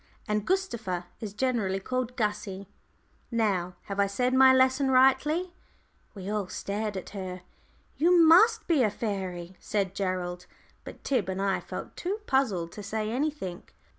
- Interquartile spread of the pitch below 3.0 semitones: No, wide, 5.5 semitones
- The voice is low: No, high, 210 Hz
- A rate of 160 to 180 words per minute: No, average, 150 wpm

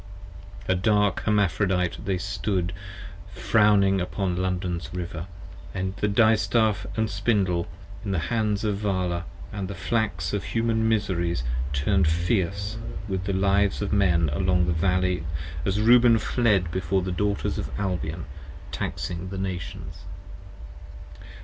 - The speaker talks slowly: Yes, slow, 130 wpm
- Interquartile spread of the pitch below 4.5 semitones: Yes, narrow, 2.6 semitones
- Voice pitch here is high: No, very low, 95 Hz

